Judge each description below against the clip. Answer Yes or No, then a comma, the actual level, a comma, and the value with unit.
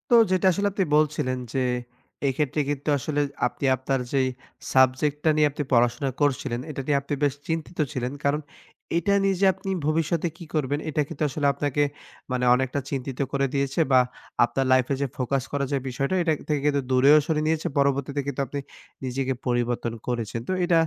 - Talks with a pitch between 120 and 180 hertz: Yes, medium, 140 Hz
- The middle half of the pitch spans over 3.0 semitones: No, average, 2.7 semitones